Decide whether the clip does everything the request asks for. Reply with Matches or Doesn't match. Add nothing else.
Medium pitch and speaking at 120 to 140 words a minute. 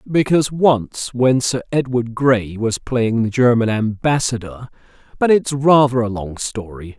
Doesn't match